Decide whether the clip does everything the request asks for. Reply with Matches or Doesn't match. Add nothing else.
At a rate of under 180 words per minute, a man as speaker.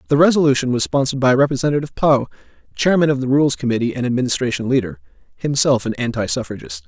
Matches